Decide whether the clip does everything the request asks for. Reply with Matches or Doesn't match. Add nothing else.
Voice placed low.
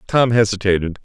Matches